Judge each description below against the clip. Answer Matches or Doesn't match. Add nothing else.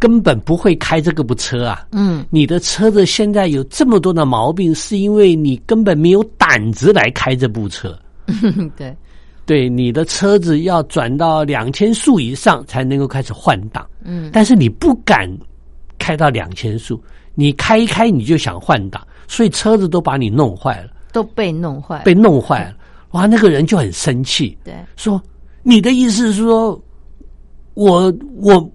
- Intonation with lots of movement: Matches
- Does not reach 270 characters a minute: Matches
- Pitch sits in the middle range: Matches